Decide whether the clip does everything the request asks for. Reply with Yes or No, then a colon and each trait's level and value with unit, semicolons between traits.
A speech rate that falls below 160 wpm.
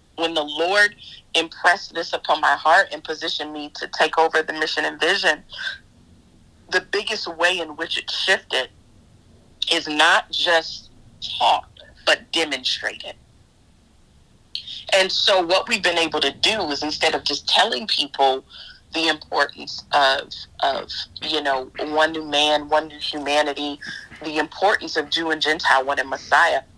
Yes: average, 150 wpm